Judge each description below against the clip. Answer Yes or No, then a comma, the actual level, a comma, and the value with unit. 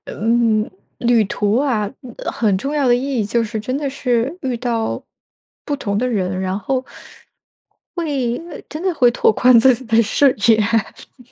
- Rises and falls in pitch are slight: No, average, 3.4 semitones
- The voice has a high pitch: Yes, high, 240 Hz